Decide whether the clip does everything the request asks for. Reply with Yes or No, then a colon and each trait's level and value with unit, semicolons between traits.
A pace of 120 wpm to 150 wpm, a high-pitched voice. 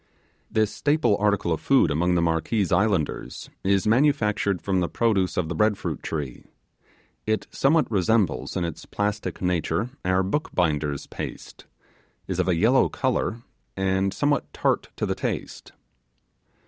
No: average, 145 wpm; very low, 95 Hz